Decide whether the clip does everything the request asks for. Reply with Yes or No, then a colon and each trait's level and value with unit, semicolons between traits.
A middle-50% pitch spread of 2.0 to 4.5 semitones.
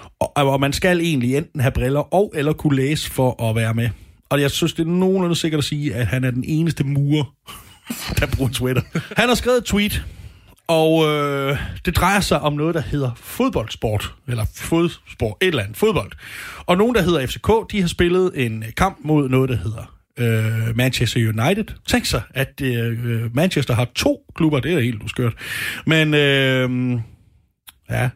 No: wide, 5.6 semitones